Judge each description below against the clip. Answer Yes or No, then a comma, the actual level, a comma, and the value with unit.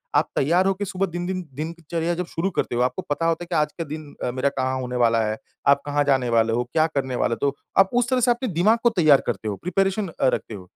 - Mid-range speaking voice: Yes, medium, 155 Hz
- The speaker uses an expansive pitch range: Yes, wide, 6.0 semitones